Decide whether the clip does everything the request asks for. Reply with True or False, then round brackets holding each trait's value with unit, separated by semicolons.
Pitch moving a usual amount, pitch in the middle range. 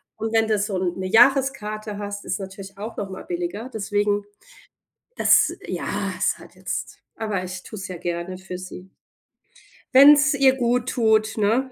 False (4.1 semitones; 210 Hz)